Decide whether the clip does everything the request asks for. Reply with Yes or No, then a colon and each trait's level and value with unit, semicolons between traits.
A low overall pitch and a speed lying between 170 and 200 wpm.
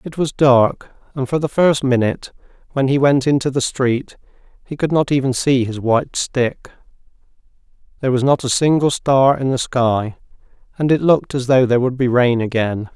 Yes: low, 130 Hz; average, 190 wpm